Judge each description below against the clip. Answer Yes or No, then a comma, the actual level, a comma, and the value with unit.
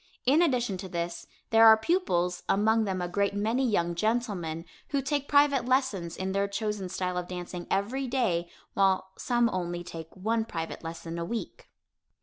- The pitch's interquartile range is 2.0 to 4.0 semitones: No, average, 5.2 semitones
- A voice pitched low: No, high, 200 Hz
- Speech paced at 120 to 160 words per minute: No, average, 170 wpm